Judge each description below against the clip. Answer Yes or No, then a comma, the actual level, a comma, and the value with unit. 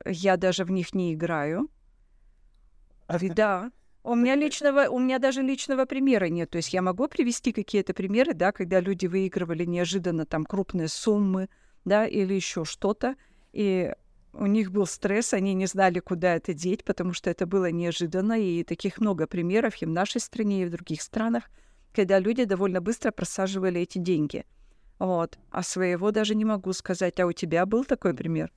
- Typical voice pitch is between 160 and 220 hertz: Yes, high, 190 Hz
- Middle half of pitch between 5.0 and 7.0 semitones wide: No, average, 3.4 semitones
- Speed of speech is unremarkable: No, fast, 175 wpm